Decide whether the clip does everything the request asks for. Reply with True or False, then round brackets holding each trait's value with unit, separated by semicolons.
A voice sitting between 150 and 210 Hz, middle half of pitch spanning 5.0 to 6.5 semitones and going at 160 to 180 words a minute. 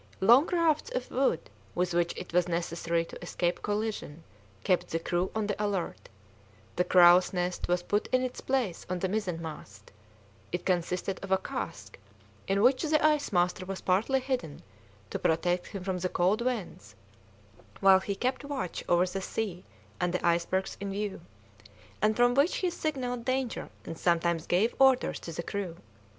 True (190 Hz; 5.6 semitones; 170 wpm)